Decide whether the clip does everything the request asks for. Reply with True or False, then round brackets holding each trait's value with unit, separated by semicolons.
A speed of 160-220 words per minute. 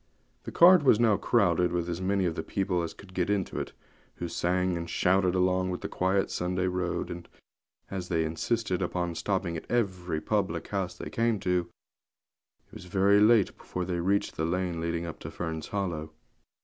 True (190 wpm)